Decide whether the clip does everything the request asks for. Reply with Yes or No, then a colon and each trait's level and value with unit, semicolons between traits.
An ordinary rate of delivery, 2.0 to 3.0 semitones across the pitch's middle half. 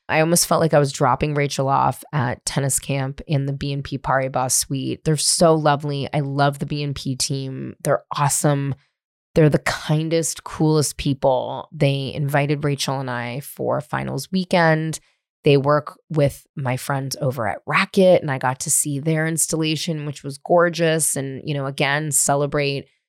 Yes: average, 165 wpm; narrow, 2.4 semitones